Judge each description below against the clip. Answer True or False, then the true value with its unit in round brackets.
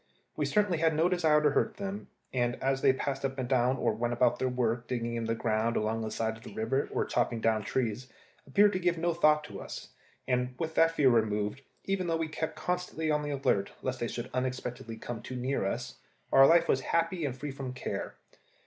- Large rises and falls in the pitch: False (5.0 semitones)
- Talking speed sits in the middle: False (230 wpm)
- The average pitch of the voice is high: False (130 Hz)